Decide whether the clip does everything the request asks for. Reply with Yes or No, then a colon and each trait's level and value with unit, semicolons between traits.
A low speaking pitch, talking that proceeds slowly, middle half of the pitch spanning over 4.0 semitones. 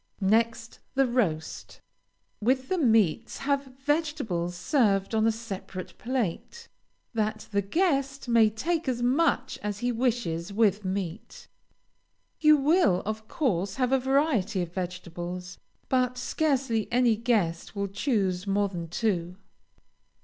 No: high, 225 Hz; slow, 125 wpm; wide, 5.5 semitones